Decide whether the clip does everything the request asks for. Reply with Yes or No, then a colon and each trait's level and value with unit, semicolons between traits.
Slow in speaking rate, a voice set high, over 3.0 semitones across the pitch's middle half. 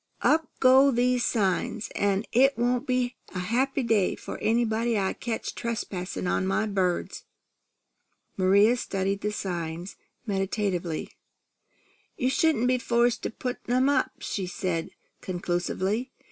Yes: slow, 130 wpm; high, 220 Hz; average, 4.6 semitones